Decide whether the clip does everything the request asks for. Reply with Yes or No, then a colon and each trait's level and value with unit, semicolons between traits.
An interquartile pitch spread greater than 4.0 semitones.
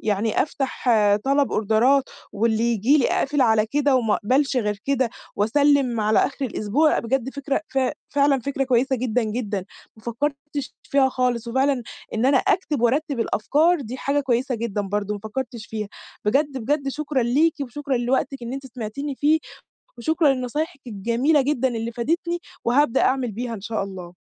No: average, 3.7 semitones